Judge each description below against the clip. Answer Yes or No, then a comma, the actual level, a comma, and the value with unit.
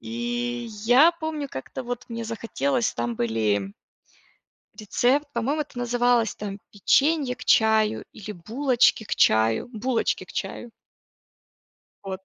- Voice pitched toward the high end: Yes, high, 235 Hz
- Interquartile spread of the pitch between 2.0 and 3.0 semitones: No, average, 3.4 semitones